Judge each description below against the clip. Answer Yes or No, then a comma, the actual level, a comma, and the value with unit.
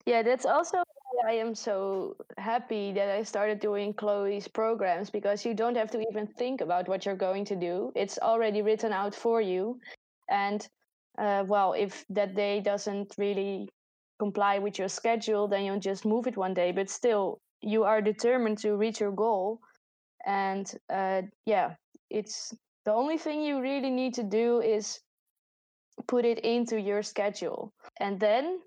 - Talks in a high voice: Yes, high, 210 Hz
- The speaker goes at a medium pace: Yes, average, 170 wpm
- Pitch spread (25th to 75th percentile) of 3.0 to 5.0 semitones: No, narrow, 2.4 semitones